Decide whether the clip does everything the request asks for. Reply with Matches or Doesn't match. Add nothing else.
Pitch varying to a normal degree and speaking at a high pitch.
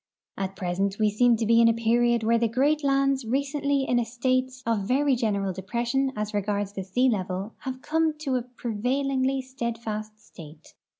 Matches